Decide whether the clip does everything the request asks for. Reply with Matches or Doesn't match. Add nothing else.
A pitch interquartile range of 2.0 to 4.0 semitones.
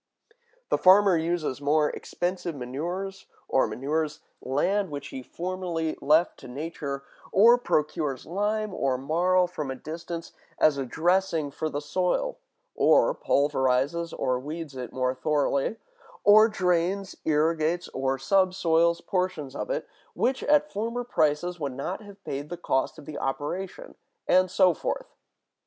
Doesn't match